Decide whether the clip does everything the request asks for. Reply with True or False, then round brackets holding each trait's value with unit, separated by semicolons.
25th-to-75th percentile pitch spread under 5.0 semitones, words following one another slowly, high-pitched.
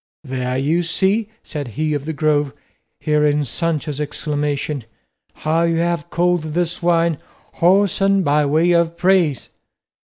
False (2.7 semitones; 130 wpm; 155 Hz)